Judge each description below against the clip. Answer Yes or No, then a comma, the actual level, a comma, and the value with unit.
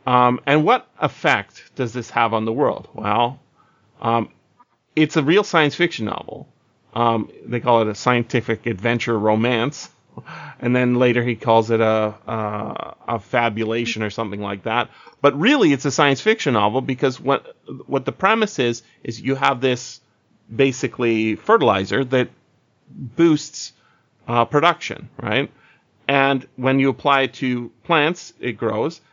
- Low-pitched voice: Yes, low, 125 Hz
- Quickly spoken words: No, average, 150 wpm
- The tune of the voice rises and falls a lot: No, average, 3.3 semitones